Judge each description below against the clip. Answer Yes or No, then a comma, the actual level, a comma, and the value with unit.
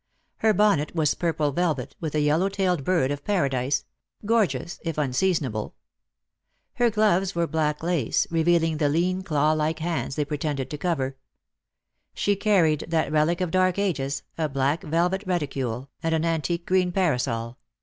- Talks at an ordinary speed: Yes, average, 160 wpm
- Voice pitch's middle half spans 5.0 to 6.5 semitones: No, average, 3.8 semitones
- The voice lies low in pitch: No, medium, 160 Hz